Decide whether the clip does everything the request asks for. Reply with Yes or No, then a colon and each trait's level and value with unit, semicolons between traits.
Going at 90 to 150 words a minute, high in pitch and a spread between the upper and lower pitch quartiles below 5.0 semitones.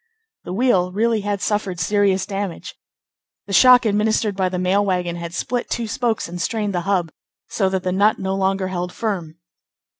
No: average, 180 wpm; high, 195 Hz; narrow, 2.5 semitones